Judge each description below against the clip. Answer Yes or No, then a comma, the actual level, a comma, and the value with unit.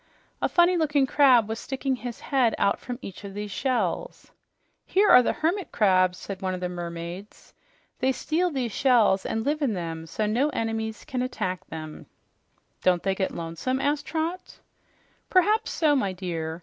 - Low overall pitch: No, high, 225 Hz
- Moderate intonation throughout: No, wide, 7.2 semitones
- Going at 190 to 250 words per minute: No, average, 175 wpm